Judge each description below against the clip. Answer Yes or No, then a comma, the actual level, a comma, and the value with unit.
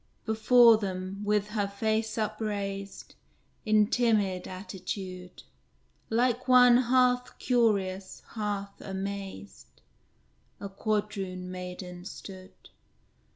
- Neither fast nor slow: No, slow, 85 wpm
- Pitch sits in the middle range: No, high, 205 Hz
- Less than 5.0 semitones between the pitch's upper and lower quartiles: Yes, average, 2.7 semitones